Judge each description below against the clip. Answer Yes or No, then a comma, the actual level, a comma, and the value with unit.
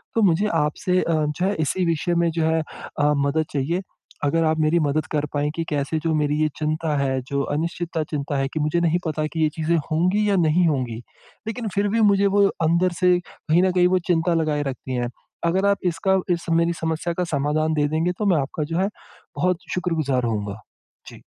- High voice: No, medium, 160 Hz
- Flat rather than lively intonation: No, average, 3.1 semitones